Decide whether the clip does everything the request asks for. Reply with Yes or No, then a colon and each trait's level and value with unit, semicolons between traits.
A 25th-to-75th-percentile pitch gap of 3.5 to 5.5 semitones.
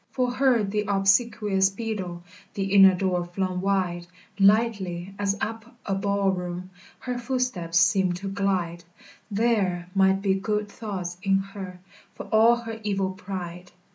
No: narrow, 2.5 semitones